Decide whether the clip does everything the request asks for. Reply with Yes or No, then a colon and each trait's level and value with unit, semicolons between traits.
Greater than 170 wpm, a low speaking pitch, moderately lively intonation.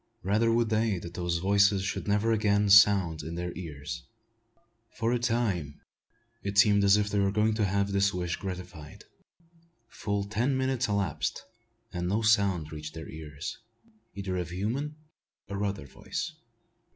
No: average, 155 wpm; low, 100 Hz; average, 3.3 semitones